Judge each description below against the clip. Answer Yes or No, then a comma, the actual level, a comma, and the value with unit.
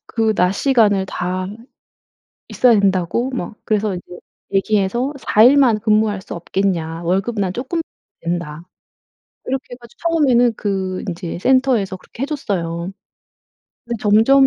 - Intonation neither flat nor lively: Yes, average, 4.8 semitones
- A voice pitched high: Yes, high, 210 Hz